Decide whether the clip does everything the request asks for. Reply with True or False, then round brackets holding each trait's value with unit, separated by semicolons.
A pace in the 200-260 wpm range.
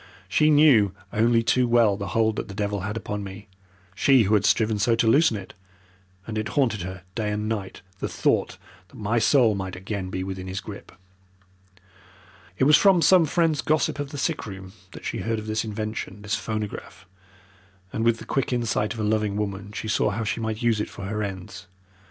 True (205 wpm)